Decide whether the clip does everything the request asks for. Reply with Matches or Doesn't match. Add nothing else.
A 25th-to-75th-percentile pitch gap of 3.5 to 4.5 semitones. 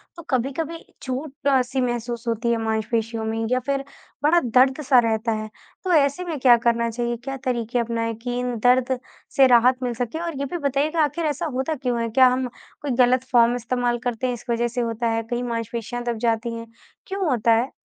Doesn't match